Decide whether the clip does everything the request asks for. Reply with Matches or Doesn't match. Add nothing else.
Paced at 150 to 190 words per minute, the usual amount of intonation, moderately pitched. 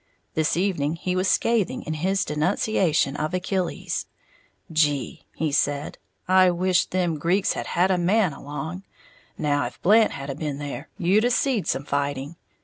Matches